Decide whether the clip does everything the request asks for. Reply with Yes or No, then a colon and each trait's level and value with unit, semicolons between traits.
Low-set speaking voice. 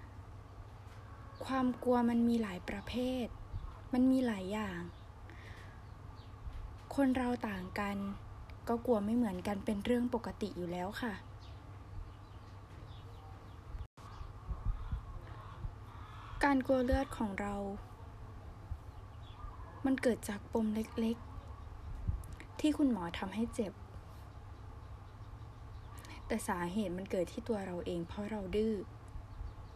Yes: low, 105 Hz